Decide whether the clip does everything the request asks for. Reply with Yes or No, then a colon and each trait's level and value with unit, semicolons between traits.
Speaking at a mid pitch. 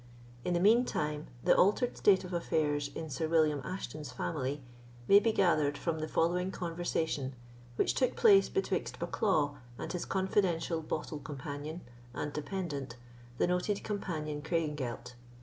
Yes: medium, 160 Hz